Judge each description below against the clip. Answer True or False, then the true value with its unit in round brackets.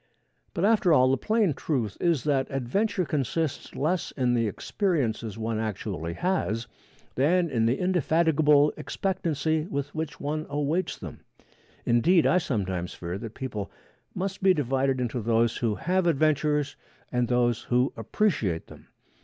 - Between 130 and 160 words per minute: True (145 wpm)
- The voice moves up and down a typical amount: False (6.2 semitones)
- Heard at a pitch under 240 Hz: True (140 Hz)